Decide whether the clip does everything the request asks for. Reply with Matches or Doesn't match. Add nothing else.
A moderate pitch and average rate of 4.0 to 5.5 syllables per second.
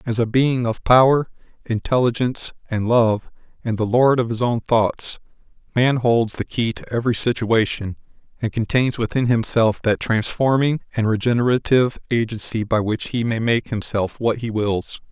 Doesn't match